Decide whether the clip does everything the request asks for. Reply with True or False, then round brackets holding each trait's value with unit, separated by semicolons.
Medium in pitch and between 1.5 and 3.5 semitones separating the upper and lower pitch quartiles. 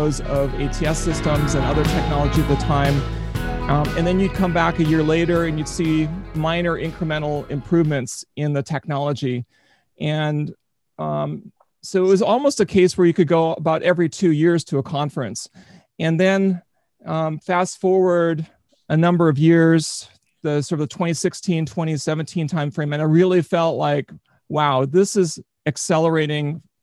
True (160 Hz; 2.6 semitones)